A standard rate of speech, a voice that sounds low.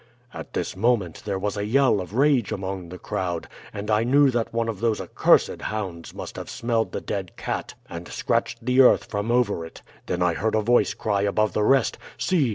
No: fast, 210 wpm; low, 105 Hz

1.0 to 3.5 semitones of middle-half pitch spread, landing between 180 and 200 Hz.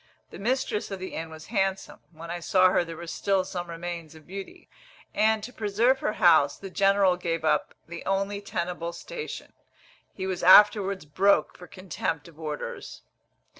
Yes: average, 2.9 semitones; medium, 185 Hz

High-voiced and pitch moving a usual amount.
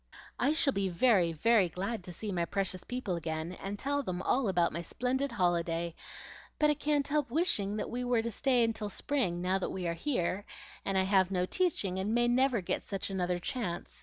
No: high, 200 Hz; wide, 5.7 semitones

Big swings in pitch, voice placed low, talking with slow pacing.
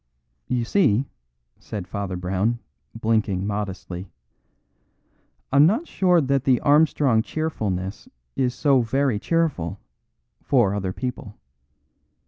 Yes: wide, 6.1 semitones; low, 115 Hz; slow, 105 wpm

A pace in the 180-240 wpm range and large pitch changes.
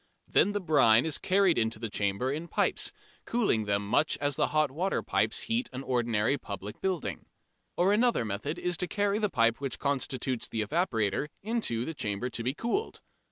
Yes: average, 185 wpm; wide, 8.1 semitones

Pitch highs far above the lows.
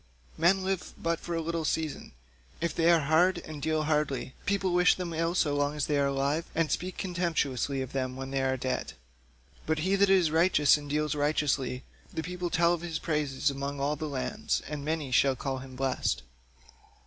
No: average, 3.4 semitones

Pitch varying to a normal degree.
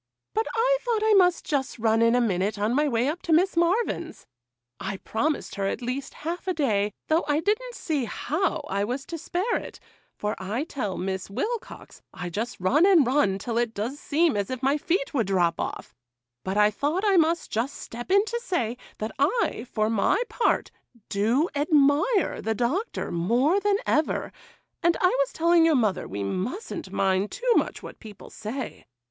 No: wide, 8.2 semitones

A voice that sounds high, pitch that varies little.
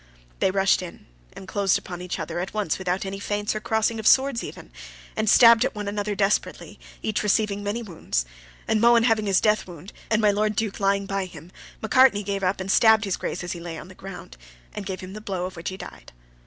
Yes: high, 200 Hz; narrow, 2.3 semitones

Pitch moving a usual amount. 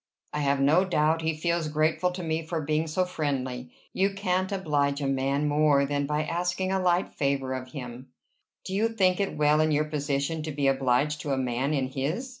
Yes: average, 3.7 semitones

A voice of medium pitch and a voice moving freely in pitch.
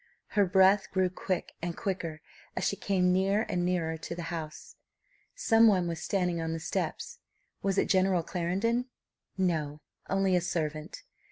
No: medium, 180 Hz; narrow, 2.6 semitones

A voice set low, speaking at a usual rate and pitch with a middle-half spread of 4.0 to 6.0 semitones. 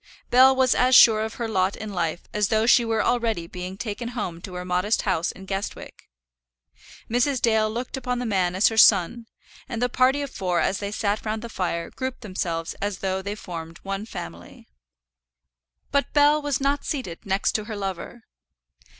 No: high, 215 Hz; average, 195 wpm; average, 4.6 semitones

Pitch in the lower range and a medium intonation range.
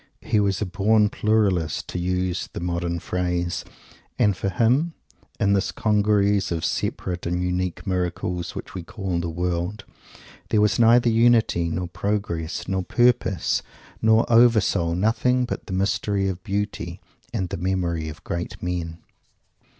Yes: very low, 95 Hz; average, 3.4 semitones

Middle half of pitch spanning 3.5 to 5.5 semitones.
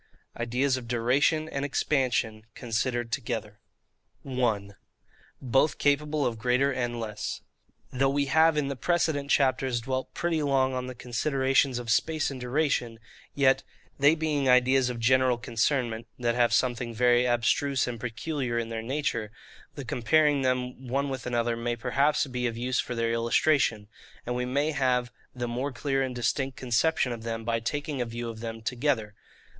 No: average, 2.9 semitones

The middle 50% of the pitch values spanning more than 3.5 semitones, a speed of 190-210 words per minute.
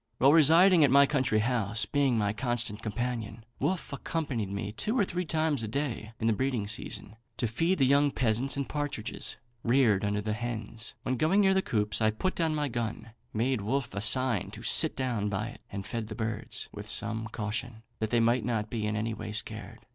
Yes: average, 4.3 semitones; fast, 205 wpm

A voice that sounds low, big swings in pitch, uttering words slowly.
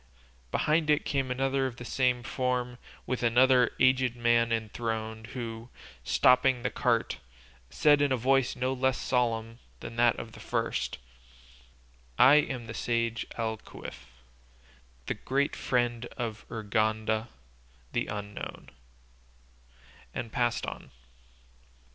No: low, 120 Hz; narrow, 2.4 semitones; slow, 120 wpm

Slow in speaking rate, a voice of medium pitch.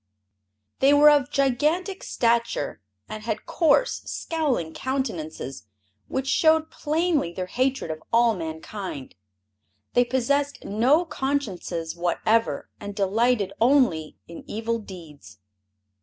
No: slow, 110 wpm; high, 235 Hz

